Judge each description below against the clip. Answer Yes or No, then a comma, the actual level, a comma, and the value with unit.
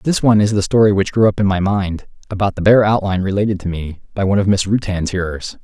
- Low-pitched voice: Yes, low, 100 Hz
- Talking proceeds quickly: Yes, fast, 255 wpm